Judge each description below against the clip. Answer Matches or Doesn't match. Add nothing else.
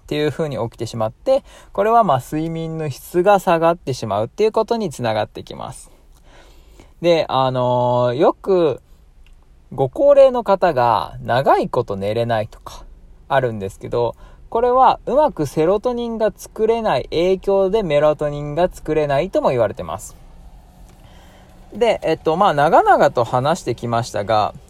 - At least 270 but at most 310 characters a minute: Matches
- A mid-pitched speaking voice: Matches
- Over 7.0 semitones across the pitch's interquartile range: Matches